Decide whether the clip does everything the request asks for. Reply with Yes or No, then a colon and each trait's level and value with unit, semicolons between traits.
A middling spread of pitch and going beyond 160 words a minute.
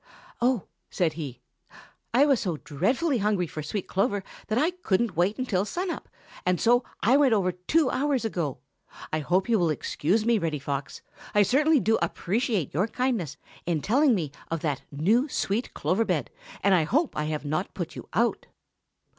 No: wide, 7.0 semitones; average, 180 wpm